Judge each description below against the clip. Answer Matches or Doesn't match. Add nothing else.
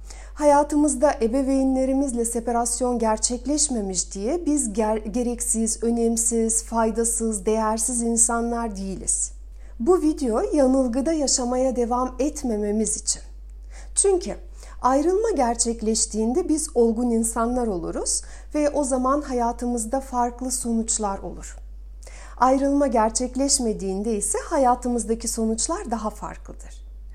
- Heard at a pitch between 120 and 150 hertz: Doesn't match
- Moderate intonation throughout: Matches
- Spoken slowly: Matches